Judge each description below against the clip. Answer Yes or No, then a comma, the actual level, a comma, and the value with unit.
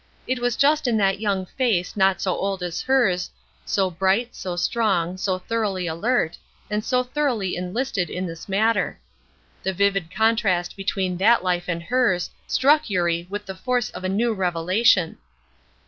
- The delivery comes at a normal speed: Yes, average, 165 wpm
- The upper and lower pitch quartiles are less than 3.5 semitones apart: No, average, 4.3 semitones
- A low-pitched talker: No, high, 195 Hz